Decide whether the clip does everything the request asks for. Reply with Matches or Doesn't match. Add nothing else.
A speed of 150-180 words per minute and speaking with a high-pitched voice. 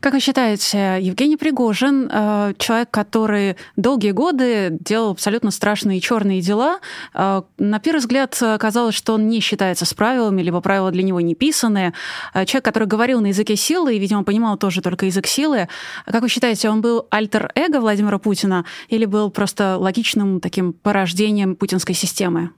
Matches